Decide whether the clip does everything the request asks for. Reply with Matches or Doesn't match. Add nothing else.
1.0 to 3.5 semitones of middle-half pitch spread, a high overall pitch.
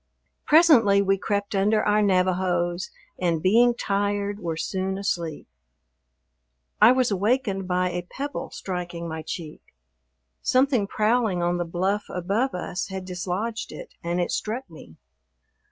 Matches